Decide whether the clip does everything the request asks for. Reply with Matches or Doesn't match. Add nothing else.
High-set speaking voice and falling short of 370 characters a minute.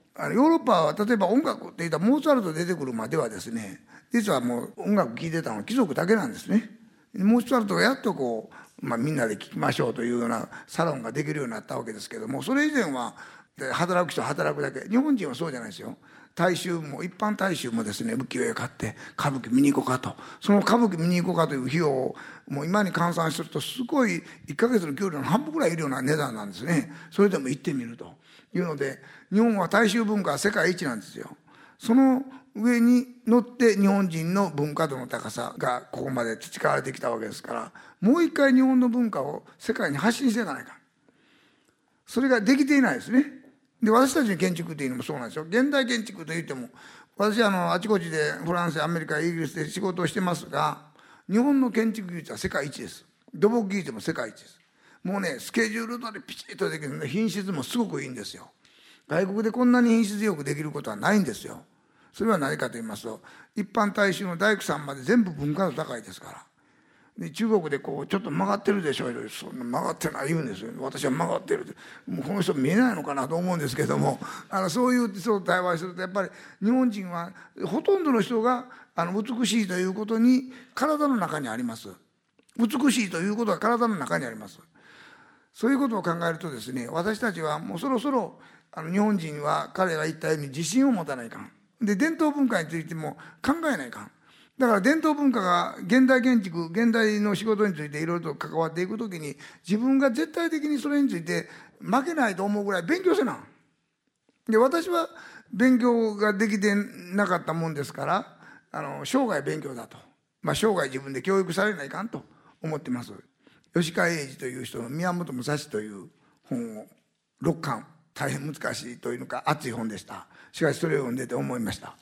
Doesn't match